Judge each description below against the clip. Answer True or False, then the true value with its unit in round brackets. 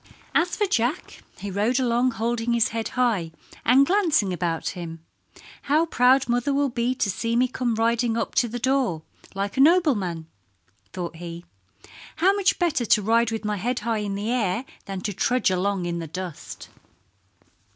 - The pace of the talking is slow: False (170 wpm)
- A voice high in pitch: True (230 Hz)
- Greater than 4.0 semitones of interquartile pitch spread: True (4.7 semitones)